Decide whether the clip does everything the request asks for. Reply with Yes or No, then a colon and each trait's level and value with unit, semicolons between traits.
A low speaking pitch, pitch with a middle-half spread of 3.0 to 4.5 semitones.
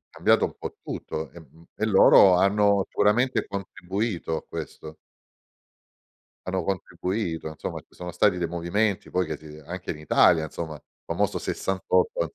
Yes: very low, 90 Hz; average, 3.6 semitones